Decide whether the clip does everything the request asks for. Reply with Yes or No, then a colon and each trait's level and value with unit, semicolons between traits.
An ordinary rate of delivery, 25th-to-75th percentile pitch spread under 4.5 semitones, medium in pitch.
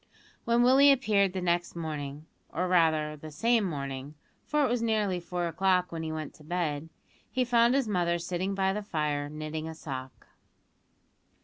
No: average, 170 wpm; average, 5.3 semitones; medium, 175 Hz